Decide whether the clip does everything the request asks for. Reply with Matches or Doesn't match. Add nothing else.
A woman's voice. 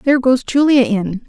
Matches